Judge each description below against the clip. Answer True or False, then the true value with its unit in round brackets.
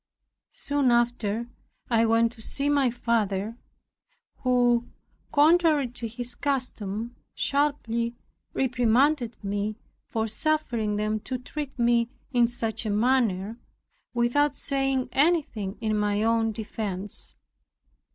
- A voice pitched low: False (235 Hz)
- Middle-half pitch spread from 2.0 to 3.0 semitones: False (3.4 semitones)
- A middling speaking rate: False (110 wpm)